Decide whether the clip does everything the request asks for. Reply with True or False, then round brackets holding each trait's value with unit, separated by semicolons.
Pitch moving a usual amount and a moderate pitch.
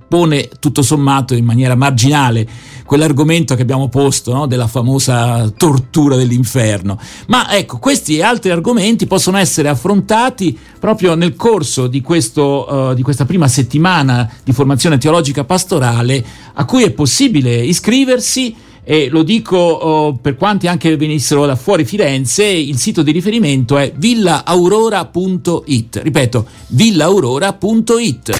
False (5.7 semitones; 150 Hz)